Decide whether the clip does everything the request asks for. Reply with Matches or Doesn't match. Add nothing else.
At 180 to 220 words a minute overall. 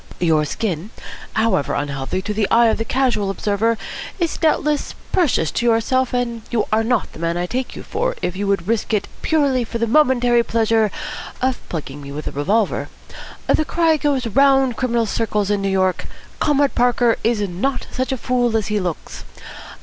Matches